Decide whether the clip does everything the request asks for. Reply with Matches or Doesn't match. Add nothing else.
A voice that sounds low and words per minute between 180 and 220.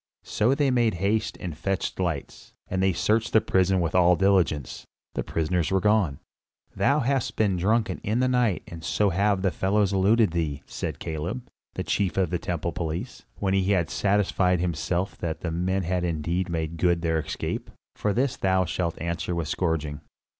Matches